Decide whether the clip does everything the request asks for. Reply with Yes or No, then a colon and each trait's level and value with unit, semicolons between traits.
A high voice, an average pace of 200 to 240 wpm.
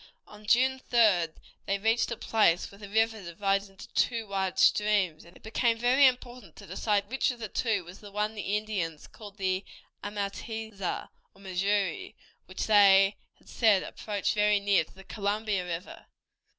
No: high, 205 Hz; average, 175 wpm